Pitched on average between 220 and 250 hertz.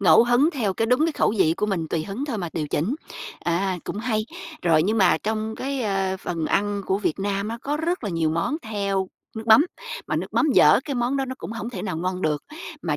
No: high, 205 Hz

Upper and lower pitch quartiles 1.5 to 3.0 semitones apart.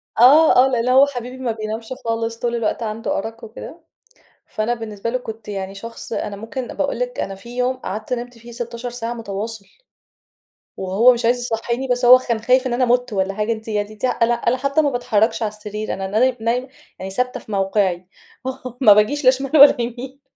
Yes: average, 2.7 semitones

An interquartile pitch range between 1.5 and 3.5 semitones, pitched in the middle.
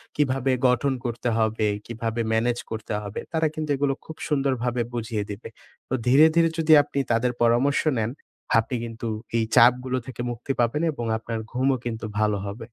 No: average, 3.1 semitones; low, 120 Hz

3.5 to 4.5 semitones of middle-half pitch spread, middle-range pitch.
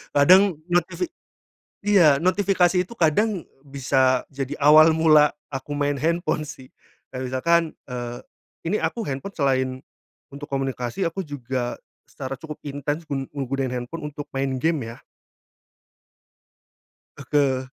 Yes: average, 3.9 semitones; medium, 145 Hz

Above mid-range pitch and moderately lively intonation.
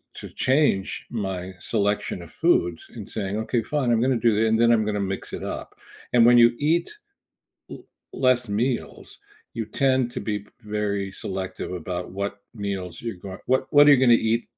No: low, 110 Hz; average, 4.0 semitones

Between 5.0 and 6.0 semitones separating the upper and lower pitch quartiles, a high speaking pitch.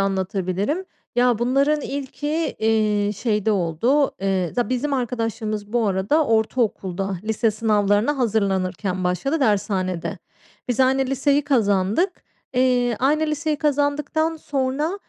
Yes: wide, 5.6 semitones; high, 230 Hz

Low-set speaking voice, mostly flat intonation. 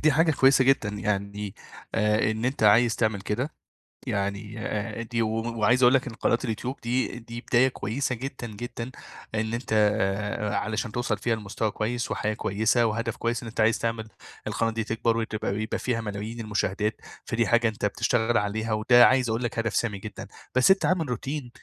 Yes: low, 115 Hz; narrow, 2.2 semitones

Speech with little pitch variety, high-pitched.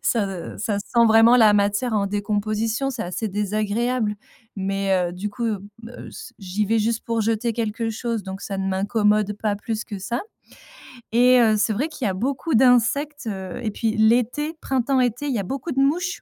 No: average, 3.1 semitones; high, 220 Hz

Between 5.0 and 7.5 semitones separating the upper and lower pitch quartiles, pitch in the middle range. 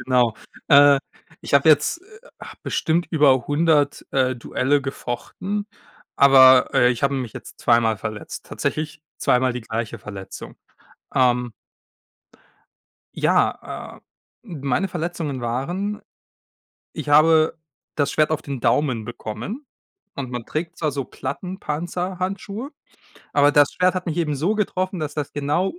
Yes: average, 5.3 semitones; medium, 145 Hz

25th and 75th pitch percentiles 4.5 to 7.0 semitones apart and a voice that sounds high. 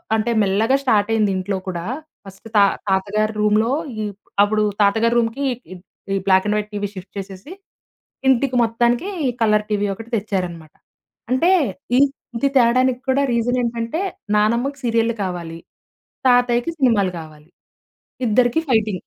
No: average, 3.3 semitones; high, 220 Hz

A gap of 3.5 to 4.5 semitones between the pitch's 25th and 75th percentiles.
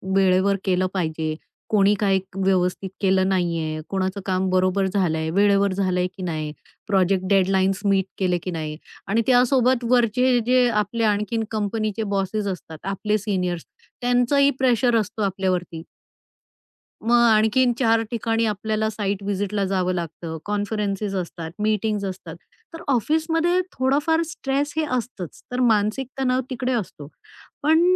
Yes: average, 3.8 semitones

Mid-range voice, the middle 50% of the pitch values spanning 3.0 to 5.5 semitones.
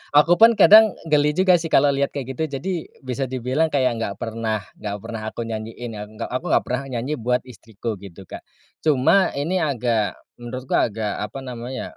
No: low, 125 Hz; average, 4.6 semitones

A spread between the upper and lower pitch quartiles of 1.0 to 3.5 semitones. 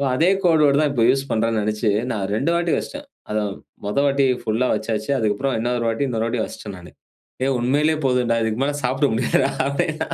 No: average, 4.0 semitones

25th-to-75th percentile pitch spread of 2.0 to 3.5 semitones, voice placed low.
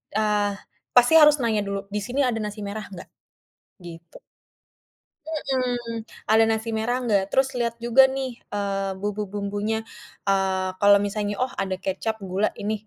No: average, 3.1 semitones; high, 210 Hz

